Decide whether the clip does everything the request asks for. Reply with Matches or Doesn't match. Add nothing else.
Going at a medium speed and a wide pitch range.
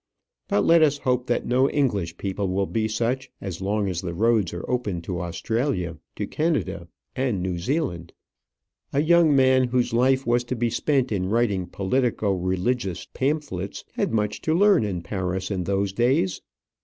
Matches